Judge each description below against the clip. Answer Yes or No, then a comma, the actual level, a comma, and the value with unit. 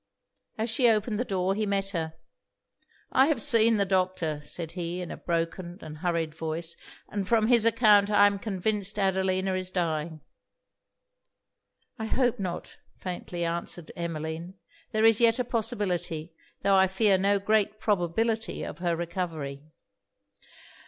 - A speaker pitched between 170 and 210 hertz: Yes, high, 190 Hz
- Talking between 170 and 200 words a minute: No, average, 145 wpm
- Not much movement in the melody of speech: No, average, 4.1 semitones